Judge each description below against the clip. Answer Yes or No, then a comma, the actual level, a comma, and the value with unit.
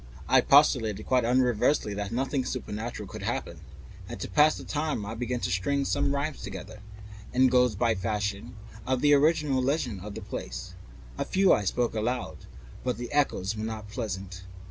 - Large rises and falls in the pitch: No, average, 4.8 semitones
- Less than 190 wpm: Yes, average, 165 wpm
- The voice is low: Yes, low, 120 Hz